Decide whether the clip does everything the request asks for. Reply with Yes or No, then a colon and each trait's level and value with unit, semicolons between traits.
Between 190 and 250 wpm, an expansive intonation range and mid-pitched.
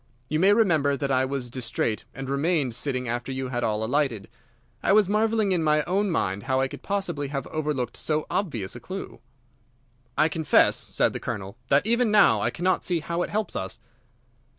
Yes: average, 195 wpm; wide, 6.2 semitones; medium, 145 Hz